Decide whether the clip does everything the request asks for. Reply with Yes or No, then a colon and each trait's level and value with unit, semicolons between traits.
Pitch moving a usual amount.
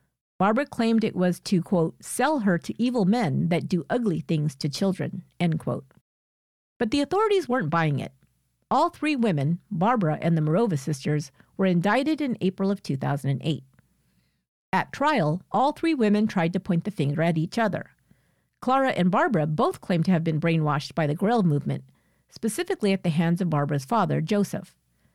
No: wide, 6.2 semitones